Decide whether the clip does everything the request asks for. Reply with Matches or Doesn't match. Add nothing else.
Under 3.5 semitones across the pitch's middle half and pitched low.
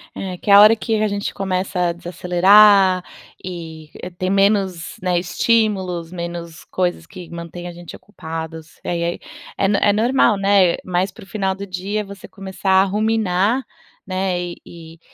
Doesn't match